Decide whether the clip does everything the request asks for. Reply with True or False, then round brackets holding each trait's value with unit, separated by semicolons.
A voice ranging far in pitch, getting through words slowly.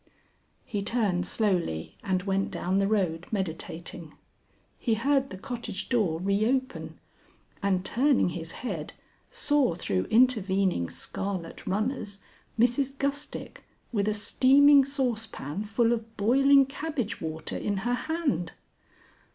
True (5.7 semitones; 120 wpm)